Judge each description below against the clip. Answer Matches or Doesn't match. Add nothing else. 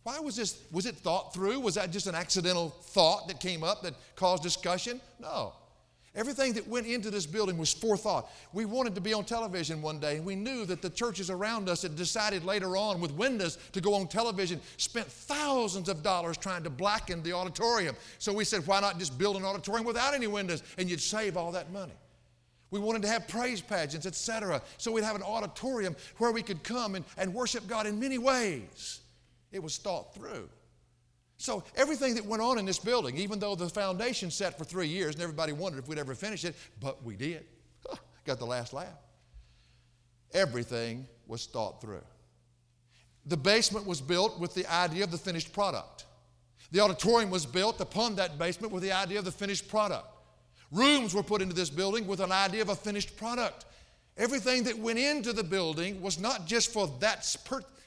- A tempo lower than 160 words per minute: Doesn't match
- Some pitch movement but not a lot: Matches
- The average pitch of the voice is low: Doesn't match